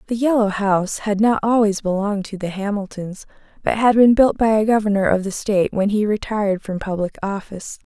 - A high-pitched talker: Yes, high, 205 Hz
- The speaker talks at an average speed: Yes, average, 195 wpm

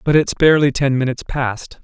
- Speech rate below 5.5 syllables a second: No, 6.0 syllables/s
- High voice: No, low, 135 Hz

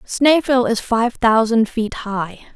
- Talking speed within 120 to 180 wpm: Yes, average, 140 wpm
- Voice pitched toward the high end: Yes, high, 230 Hz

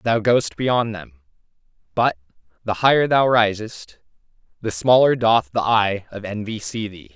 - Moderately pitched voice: No, low, 110 Hz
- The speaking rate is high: No, average, 150 wpm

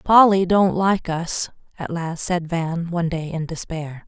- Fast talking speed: No, average, 175 wpm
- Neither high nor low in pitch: Yes, medium, 170 Hz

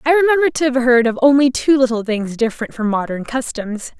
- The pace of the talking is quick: Yes, fast, 210 wpm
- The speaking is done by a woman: Yes, female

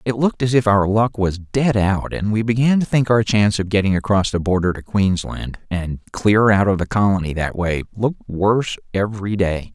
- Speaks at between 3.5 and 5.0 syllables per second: No, 5.2 syllables/s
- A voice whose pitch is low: Yes, low, 105 Hz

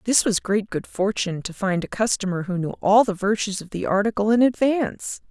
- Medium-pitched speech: No, high, 205 Hz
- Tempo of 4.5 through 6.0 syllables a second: Yes, 5.5 syllables/s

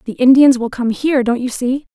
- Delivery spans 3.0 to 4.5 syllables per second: No, 5.7 syllables/s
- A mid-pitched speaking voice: No, very high, 255 Hz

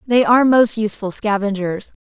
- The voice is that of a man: No, female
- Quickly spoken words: No, average, 150 wpm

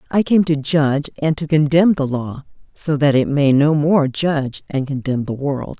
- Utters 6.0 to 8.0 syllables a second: No, 4.6 syllables/s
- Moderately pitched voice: Yes, medium, 145 Hz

